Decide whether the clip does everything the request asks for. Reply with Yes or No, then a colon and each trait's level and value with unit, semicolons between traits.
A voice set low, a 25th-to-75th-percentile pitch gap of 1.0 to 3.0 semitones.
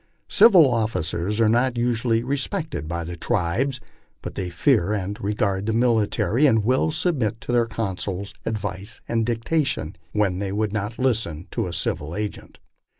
No: low, 110 Hz; average, 3.9 semitones